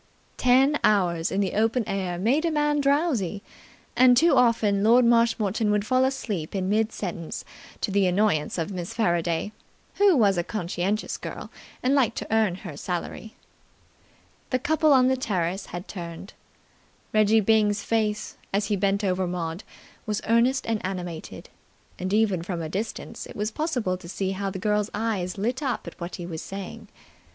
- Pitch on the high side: Yes, high, 205 Hz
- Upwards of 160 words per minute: Yes, average, 170 wpm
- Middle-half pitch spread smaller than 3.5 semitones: No, average, 4.2 semitones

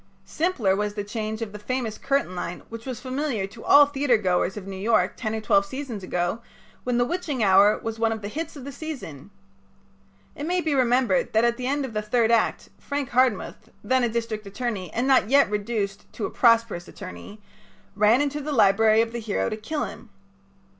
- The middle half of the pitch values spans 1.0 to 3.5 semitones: No, average, 3.9 semitones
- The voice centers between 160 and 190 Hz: No, high, 230 Hz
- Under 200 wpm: No, fast, 205 wpm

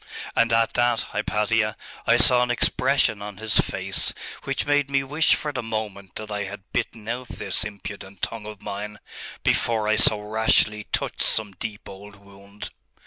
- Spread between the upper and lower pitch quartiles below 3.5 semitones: Yes, narrow, 2.4 semitones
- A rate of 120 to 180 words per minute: Yes, average, 170 wpm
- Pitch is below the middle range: Yes, low, 105 Hz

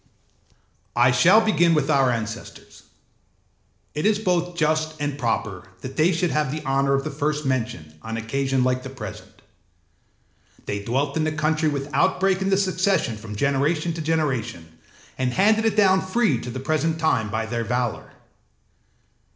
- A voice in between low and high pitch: Yes, medium, 145 Hz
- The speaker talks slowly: No, average, 165 wpm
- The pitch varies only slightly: No, average, 5.0 semitones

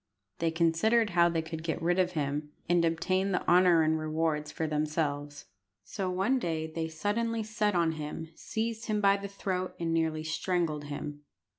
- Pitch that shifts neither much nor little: Yes, average, 3.2 semitones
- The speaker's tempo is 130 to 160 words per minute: No, average, 175 wpm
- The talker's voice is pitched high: No, medium, 165 Hz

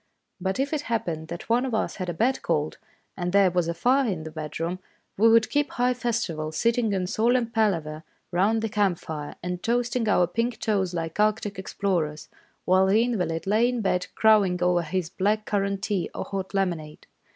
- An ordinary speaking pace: Yes, average, 195 wpm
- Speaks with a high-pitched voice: Yes, high, 195 Hz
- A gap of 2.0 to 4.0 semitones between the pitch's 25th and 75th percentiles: No, average, 4.4 semitones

